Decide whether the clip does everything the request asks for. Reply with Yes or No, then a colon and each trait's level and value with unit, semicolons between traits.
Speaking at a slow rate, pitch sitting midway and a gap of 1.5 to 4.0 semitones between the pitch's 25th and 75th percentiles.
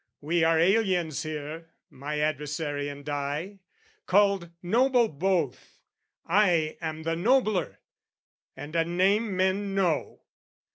No: slow, 110 wpm; medium, 170 Hz; average, 4.4 semitones